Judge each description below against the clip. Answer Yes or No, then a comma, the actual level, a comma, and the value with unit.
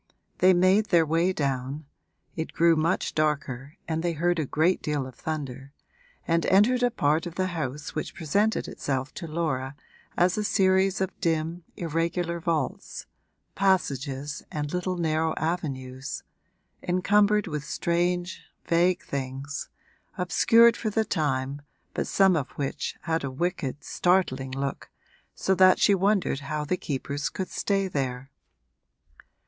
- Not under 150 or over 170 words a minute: No, average, 140 wpm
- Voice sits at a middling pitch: Yes, medium, 165 Hz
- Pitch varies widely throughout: No, average, 4.4 semitones